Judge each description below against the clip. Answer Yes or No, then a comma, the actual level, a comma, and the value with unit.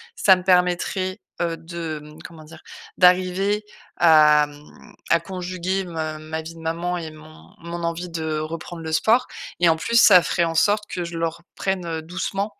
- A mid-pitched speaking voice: Yes, medium, 170 Hz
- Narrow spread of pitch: Yes, narrow, 2.3 semitones